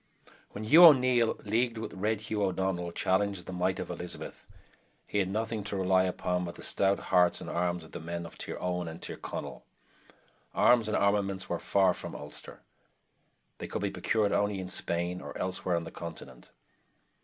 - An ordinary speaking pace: Yes, average, 185 wpm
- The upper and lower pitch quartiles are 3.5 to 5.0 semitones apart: No, average, 2.9 semitones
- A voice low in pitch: Yes, very low, 95 Hz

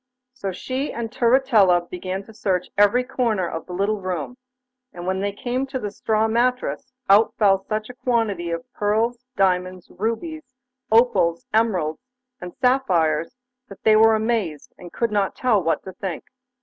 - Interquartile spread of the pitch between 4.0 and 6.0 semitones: Yes, average, 4.4 semitones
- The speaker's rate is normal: Yes, average, 160 wpm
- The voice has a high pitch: Yes, high, 210 Hz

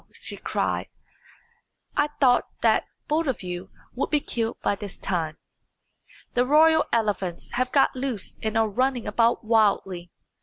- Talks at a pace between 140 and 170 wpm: Yes, average, 145 wpm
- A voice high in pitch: Yes, high, 230 Hz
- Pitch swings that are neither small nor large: Yes, average, 5.0 semitones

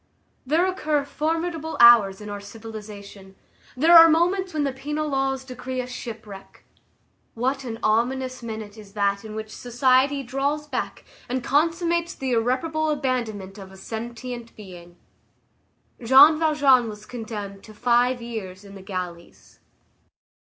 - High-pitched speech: Yes, high, 245 Hz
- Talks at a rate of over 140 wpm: No, slow, 135 wpm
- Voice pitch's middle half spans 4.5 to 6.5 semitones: Yes, average, 5.2 semitones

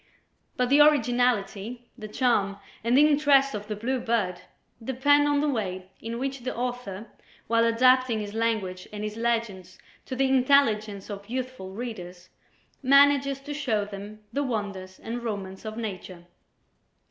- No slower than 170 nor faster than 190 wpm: No, average, 150 wpm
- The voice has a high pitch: Yes, high, 230 Hz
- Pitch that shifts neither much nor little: Yes, average, 4.1 semitones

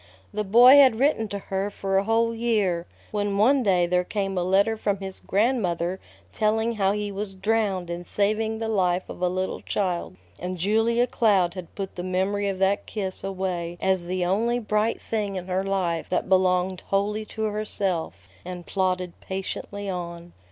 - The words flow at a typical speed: Yes, average, 180 wpm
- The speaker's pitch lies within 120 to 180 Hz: No, high, 195 Hz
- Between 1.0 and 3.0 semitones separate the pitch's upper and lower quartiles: Yes, average, 2.7 semitones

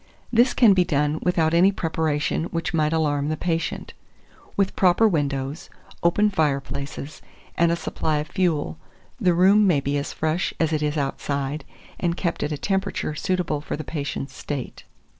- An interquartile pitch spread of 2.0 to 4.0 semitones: Yes, average, 3.5 semitones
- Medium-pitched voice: Yes, medium, 160 Hz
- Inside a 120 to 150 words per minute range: No, average, 165 wpm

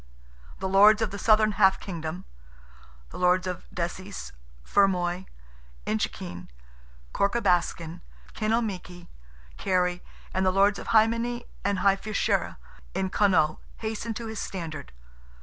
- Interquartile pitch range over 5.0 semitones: No, average, 3.4 semitones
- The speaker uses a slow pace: Yes, slow, 120 wpm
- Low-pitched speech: No, high, 190 Hz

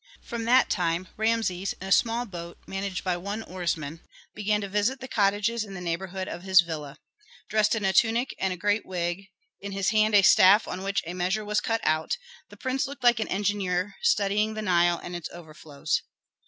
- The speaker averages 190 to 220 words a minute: Yes, average, 200 wpm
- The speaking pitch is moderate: No, high, 195 Hz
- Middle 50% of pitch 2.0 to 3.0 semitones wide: No, average, 3.4 semitones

